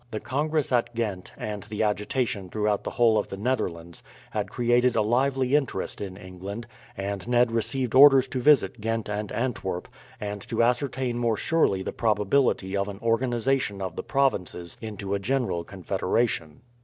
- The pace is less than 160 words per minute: No, average, 165 wpm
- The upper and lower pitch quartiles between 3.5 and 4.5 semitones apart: Yes, average, 4.0 semitones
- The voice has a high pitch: No, low, 110 Hz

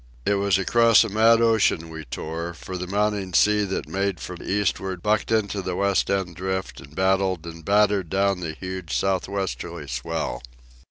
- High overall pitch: No, very low, 95 Hz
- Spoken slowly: No, average, 175 wpm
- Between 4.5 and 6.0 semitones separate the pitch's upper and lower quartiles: No, narrow, 2.6 semitones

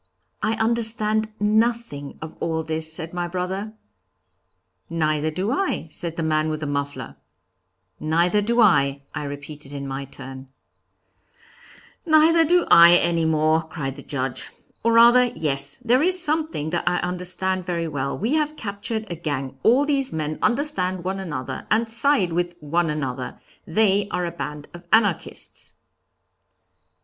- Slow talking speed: No, average, 150 wpm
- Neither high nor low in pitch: Yes, medium, 175 Hz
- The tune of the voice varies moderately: No, wide, 6.4 semitones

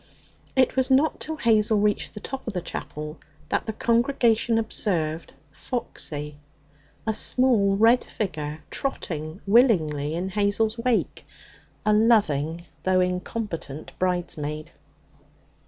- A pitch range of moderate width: No, wide, 6.3 semitones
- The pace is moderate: No, slow, 115 wpm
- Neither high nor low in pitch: No, high, 205 Hz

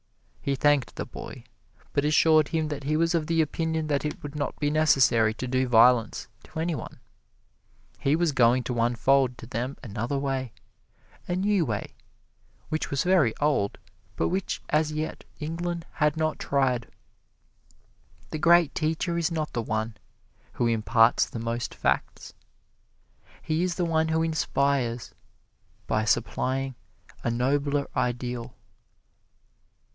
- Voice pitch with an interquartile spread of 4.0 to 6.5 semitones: Yes, average, 4.5 semitones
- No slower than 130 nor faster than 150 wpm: Yes, average, 145 wpm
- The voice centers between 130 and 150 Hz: Yes, medium, 140 Hz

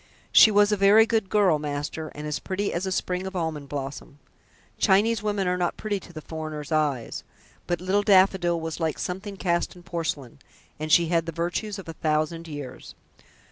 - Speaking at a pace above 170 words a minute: Yes, average, 190 wpm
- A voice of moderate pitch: Yes, medium, 175 Hz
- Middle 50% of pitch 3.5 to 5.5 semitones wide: Yes, average, 3.9 semitones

